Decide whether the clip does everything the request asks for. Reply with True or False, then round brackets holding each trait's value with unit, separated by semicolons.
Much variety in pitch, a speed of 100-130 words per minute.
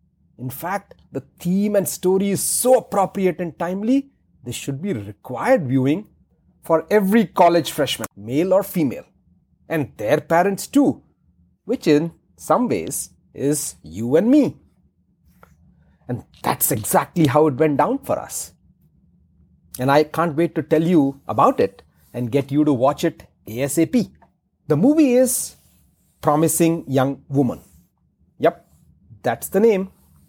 False (5.9 semitones; 140 wpm)